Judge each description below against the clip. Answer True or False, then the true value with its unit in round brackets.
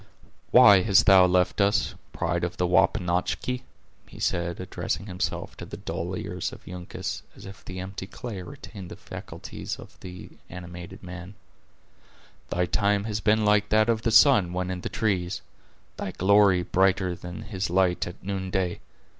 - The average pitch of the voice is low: True (95 Hz)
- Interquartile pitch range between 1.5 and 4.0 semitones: True (2.5 semitones)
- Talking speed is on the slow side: False (165 wpm)